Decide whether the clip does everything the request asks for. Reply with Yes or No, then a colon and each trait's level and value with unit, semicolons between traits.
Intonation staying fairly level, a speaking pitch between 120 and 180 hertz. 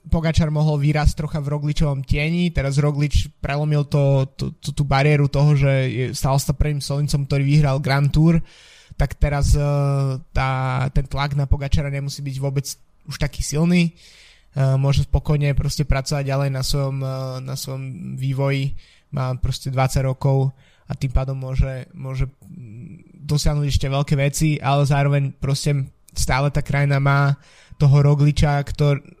Yes: narrow, 1.5 semitones; medium, 140 Hz